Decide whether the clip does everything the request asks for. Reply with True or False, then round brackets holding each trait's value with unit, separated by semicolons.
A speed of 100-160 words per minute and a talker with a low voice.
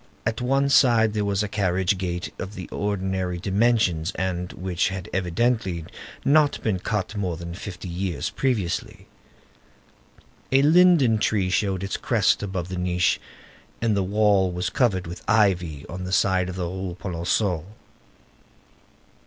True (145 wpm; 95 Hz)